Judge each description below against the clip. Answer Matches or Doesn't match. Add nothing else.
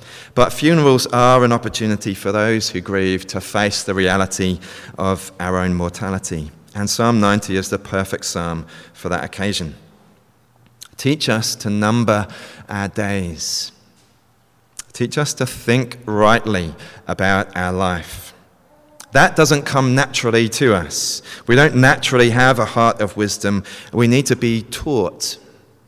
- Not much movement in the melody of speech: Doesn't match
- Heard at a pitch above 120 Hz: Doesn't match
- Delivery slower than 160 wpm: Matches